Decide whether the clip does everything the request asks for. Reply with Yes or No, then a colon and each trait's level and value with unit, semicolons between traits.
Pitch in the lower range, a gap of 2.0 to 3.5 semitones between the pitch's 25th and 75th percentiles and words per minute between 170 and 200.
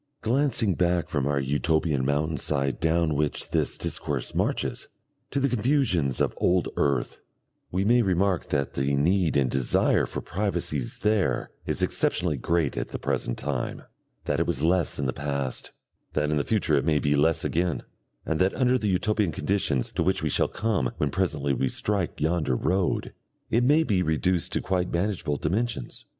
No: very low, 85 Hz; average, 5.3 semitones; average, 175 wpm